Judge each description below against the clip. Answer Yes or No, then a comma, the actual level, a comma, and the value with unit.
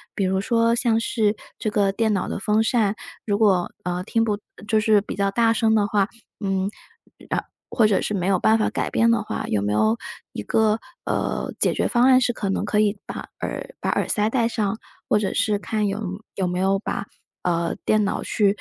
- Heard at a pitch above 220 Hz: No, high, 210 Hz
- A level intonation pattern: Yes, narrow, 2.3 semitones